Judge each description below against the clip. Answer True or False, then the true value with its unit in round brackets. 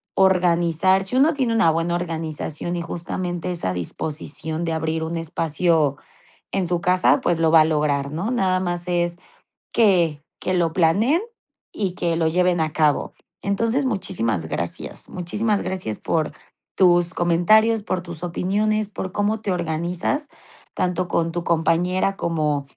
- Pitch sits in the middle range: True (175 Hz)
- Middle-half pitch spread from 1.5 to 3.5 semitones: True (2.8 semitones)